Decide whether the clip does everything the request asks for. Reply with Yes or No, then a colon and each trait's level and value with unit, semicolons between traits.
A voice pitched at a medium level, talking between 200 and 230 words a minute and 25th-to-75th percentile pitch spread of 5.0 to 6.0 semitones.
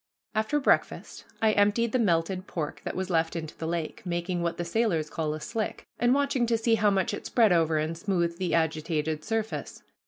Yes: medium, 180 Hz; fast, 205 wpm; average, 5.3 semitones